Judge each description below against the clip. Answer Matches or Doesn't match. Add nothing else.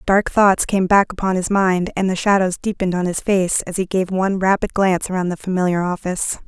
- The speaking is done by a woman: Matches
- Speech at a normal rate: Doesn't match